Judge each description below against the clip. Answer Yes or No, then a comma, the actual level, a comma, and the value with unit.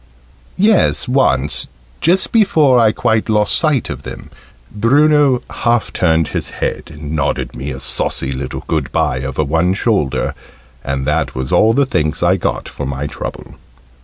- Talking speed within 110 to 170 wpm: Yes, average, 160 wpm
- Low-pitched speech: Yes, very low, 90 Hz